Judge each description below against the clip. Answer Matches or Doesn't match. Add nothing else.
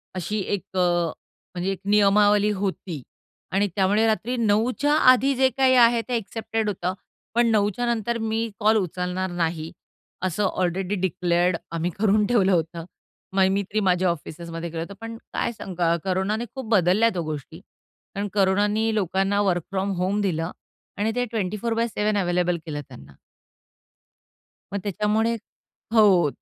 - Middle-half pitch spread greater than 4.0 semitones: Doesn't match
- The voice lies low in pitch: Doesn't match